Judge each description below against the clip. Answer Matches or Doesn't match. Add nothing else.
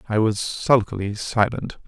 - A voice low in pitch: Matches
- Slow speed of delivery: Matches